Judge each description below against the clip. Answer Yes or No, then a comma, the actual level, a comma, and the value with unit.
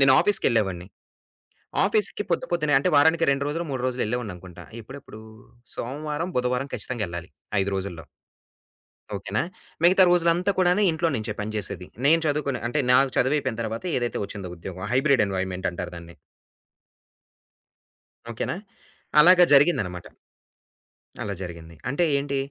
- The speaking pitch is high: No, low, 125 Hz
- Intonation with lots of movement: Yes, wide, 7.6 semitones